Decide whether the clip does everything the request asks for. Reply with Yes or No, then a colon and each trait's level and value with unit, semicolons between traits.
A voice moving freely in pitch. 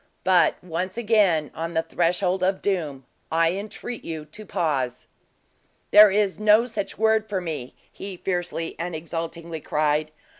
No: average, 3.9 semitones